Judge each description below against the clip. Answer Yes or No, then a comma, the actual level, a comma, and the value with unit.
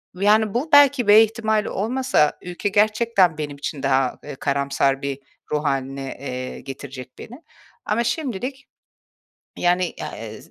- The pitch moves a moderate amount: No, wide, 8.3 semitones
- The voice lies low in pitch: No, medium, 185 Hz